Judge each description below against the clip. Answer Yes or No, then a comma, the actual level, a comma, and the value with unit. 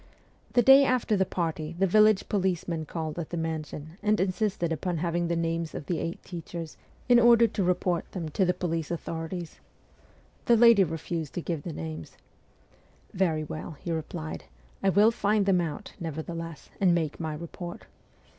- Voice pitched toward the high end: No, medium, 170 Hz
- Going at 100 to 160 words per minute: No, average, 175 wpm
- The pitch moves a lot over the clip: No, average, 3.1 semitones